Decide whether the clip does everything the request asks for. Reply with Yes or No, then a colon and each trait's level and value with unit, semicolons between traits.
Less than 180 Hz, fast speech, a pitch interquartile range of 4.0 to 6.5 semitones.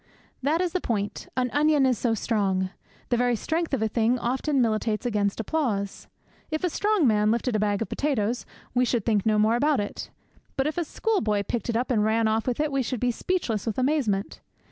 No: high, 240 Hz; fast, 215 wpm; average, 4.6 semitones